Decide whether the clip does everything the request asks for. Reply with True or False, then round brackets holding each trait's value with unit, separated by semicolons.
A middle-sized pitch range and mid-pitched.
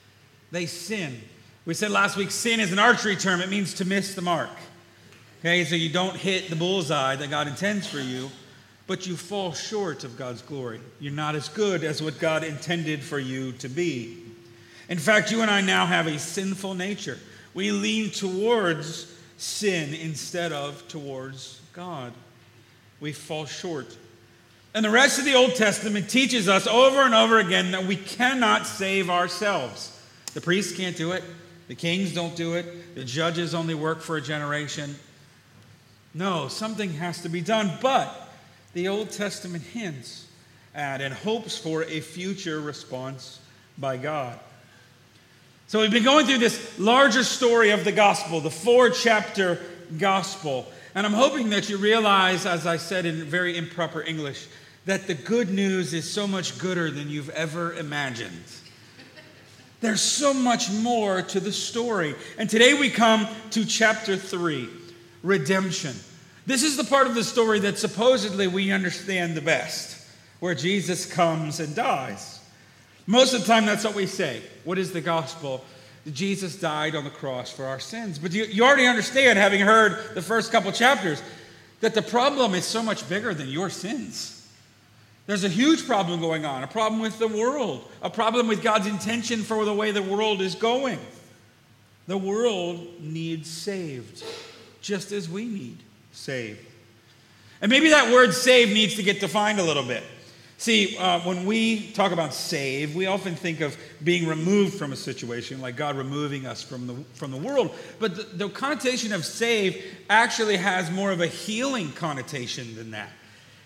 False (6.4 semitones; 175 Hz)